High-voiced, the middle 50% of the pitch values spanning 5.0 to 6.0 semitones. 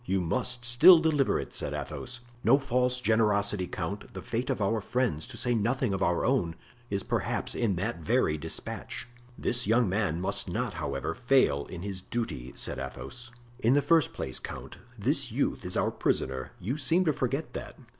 No: low, 115 Hz; wide, 5.6 semitones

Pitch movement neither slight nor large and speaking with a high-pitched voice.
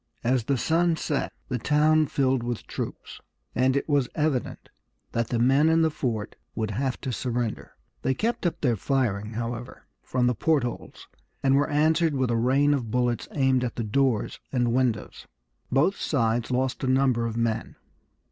No: average, 3.4 semitones; low, 130 Hz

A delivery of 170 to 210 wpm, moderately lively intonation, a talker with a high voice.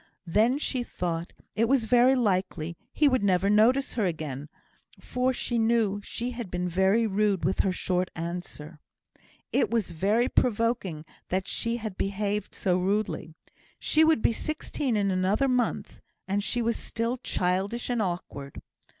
No: average, 155 wpm; average, 4.6 semitones; high, 210 Hz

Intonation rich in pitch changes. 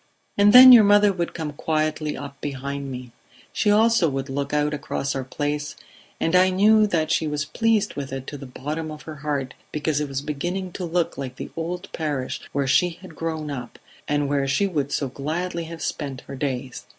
No: average, 4.1 semitones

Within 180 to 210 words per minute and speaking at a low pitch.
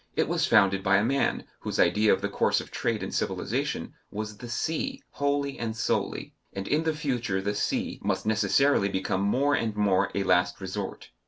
Yes: average, 190 wpm; low, 105 Hz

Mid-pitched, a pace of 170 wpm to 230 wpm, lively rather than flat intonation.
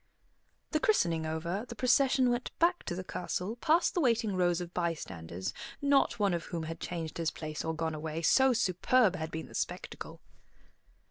Yes: medium, 180 Hz; average, 180 wpm; wide, 7.3 semitones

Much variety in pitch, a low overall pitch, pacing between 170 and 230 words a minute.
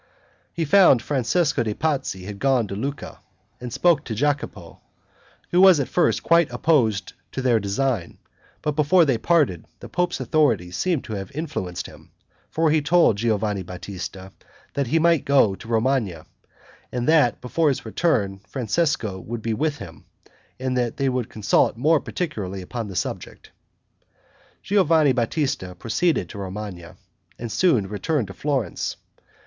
No: wide, 7.0 semitones; low, 125 Hz; average, 155 wpm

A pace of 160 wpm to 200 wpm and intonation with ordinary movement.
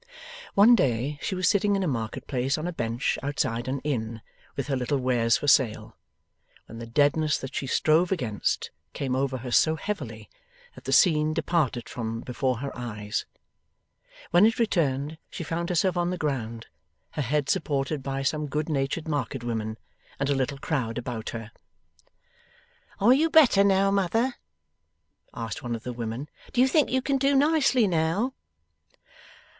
No: average, 170 wpm; wide, 6.6 semitones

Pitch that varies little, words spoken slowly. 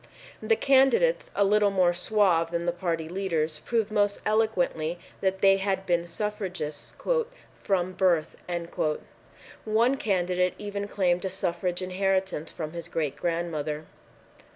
No: average, 3.1 semitones; slow, 130 wpm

